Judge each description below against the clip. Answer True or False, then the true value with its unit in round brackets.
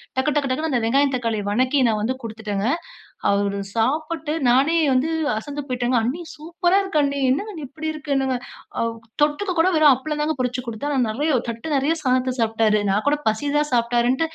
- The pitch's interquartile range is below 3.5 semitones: False (4.4 semitones)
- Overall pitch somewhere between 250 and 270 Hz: True (260 Hz)